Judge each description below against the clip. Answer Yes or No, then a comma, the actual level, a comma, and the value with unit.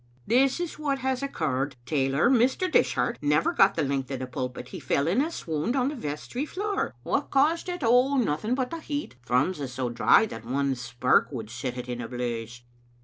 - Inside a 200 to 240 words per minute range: Yes, fast, 205 wpm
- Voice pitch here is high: No, medium, 155 Hz